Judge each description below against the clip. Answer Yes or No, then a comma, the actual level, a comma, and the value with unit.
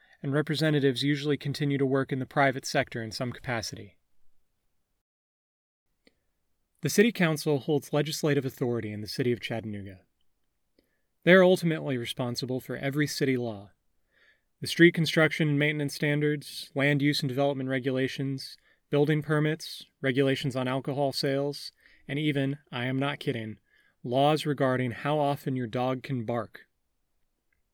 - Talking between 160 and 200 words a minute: No, slow, 135 wpm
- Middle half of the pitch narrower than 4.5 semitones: Yes, average, 3.0 semitones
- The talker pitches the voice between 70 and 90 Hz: No, medium, 140 Hz